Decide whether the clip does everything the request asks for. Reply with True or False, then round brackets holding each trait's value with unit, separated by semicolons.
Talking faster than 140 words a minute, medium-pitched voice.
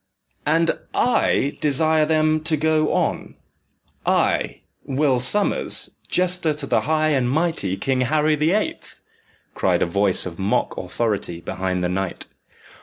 False (135 wpm; 150 Hz)